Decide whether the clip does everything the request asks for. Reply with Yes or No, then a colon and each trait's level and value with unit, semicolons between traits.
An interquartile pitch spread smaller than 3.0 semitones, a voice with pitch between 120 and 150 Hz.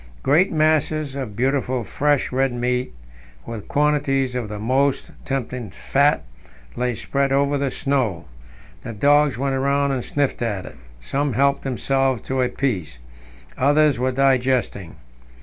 Yes: narrow, 2.4 semitones; low, 135 Hz